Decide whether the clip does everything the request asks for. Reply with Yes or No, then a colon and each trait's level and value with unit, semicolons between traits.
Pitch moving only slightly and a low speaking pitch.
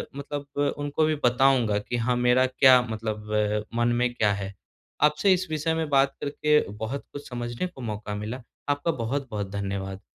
No: average, 5.0 semitones; low, 125 Hz